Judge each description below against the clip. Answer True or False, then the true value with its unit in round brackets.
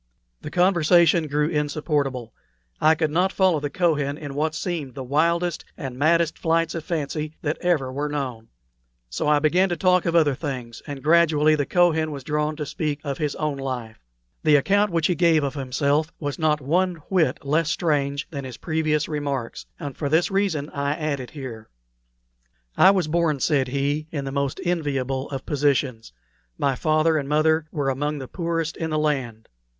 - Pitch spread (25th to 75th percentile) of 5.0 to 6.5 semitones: False (2.8 semitones)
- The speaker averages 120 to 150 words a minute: False (185 wpm)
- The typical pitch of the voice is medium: True (150 Hz)